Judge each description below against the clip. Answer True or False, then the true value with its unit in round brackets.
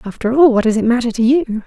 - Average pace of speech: False (290 wpm)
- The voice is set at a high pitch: True (240 Hz)